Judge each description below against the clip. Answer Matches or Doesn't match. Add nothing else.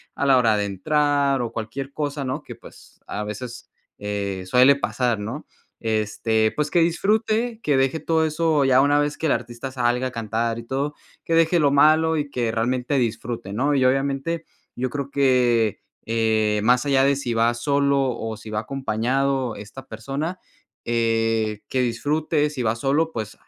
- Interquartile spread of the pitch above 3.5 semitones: Matches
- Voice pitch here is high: Doesn't match